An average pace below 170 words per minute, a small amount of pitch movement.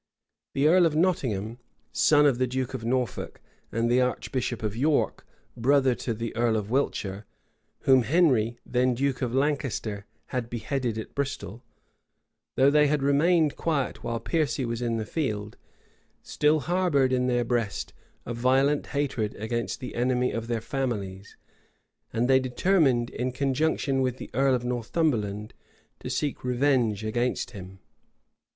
No: average, 150 wpm; average, 3.3 semitones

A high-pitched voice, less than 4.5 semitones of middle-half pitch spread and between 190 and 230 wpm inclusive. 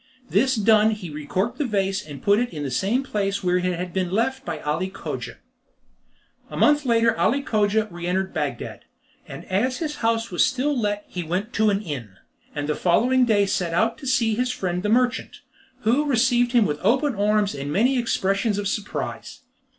No: high, 210 Hz; average, 4.9 semitones; average, 195 wpm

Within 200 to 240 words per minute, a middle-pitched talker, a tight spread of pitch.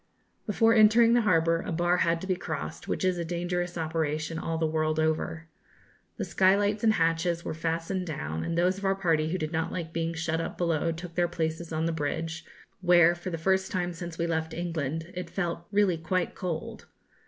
Yes: fast, 205 wpm; medium, 170 Hz; narrow, 2.0 semitones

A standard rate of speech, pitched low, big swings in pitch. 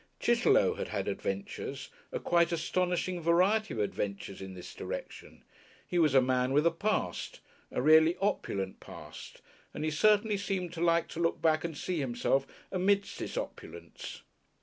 No: average, 160 wpm; medium, 165 Hz; wide, 6.0 semitones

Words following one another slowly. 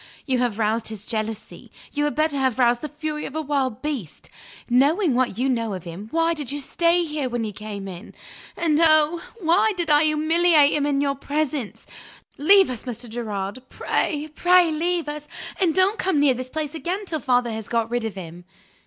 No: average, 200 wpm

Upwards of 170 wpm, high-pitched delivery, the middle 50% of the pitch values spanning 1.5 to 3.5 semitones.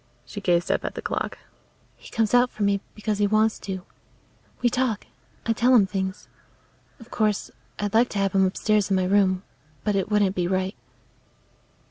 Yes: average, 185 wpm; high, 205 Hz; narrow, 2.4 semitones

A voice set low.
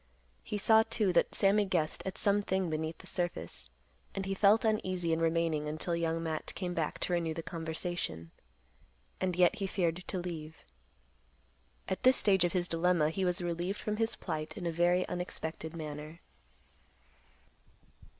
No: medium, 175 Hz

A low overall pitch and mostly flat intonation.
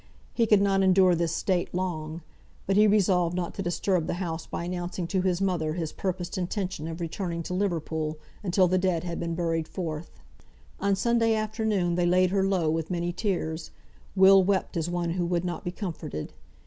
No: medium, 180 Hz; narrow, 2.3 semitones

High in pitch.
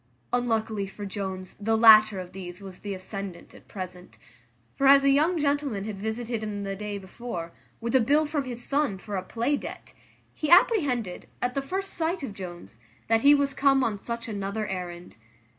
Yes: high, 220 Hz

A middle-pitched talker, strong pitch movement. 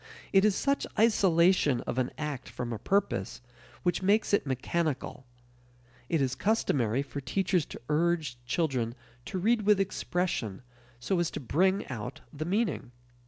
Yes: medium, 165 Hz; wide, 6.8 semitones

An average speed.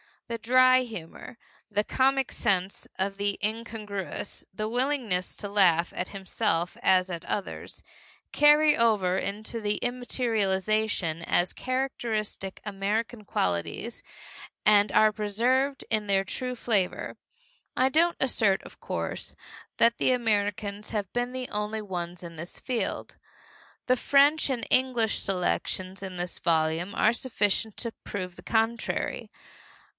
No: slow, 125 wpm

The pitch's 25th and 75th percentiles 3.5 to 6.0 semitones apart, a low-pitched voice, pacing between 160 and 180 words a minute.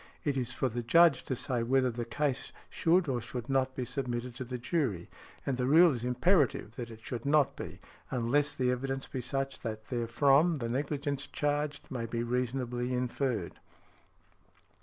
No: average, 2.7 semitones; low, 130 Hz; average, 175 wpm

